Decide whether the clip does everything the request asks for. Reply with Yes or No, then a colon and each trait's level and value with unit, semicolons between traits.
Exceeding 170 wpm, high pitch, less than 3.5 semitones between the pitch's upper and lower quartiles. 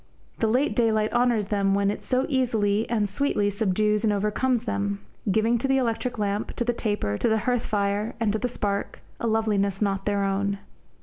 Yes: average, 195 wpm; high, 215 Hz; narrow, 2.6 semitones